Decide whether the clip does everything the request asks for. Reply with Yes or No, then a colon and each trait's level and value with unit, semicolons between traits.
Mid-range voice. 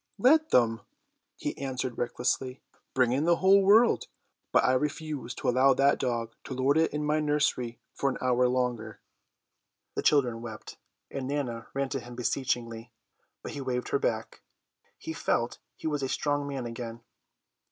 No: low, 130 Hz